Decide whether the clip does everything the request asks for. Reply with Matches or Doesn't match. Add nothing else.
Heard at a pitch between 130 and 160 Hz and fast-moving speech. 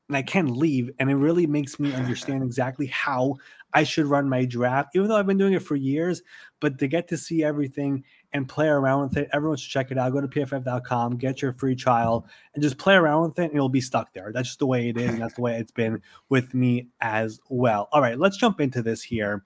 Matches